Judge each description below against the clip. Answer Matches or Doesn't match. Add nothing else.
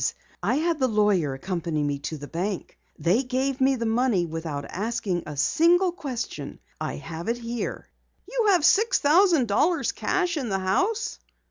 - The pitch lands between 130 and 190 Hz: Doesn't match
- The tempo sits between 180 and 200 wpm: Doesn't match